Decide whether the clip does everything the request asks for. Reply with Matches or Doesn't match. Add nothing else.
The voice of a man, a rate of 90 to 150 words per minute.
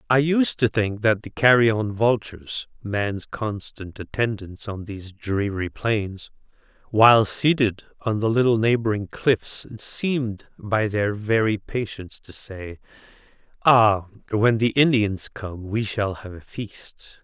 Matches